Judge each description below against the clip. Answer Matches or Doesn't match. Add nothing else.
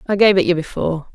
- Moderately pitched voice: Matches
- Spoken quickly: Matches